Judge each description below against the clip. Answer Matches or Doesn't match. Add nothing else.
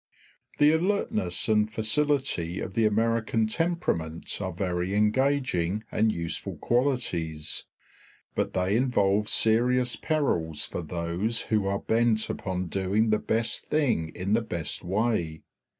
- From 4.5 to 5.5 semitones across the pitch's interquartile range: Matches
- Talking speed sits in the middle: Doesn't match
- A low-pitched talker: Matches